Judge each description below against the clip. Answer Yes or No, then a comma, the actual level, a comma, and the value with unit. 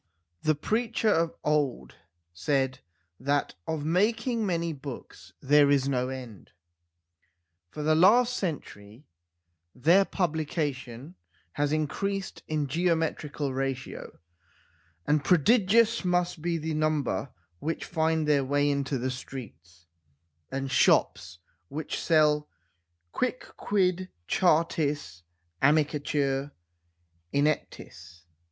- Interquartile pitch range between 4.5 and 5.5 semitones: No, average, 3.9 semitones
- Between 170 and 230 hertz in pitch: No, medium, 150 Hz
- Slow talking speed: Yes, slow, 95 wpm